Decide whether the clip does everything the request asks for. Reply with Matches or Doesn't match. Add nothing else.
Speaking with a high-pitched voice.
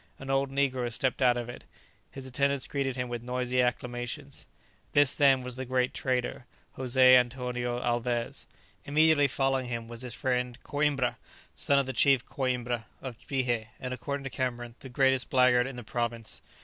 Doesn't match